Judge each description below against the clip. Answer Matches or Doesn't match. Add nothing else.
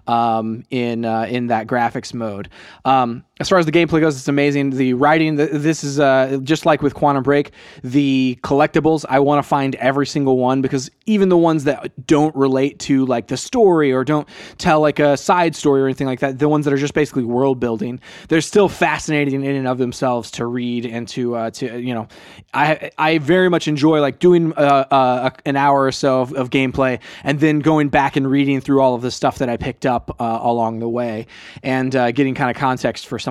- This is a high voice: Doesn't match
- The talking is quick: Matches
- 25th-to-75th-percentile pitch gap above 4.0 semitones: Doesn't match